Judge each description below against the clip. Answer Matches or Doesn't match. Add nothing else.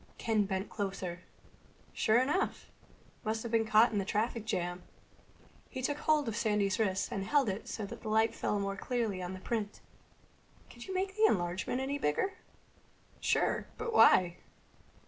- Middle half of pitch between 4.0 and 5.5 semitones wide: Matches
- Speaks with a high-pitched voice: Matches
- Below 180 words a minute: Matches